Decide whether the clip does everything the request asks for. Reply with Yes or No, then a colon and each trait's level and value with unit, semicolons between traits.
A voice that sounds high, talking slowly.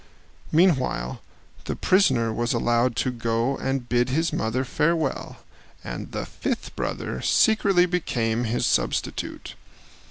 No: low, 125 Hz; slow, 120 wpm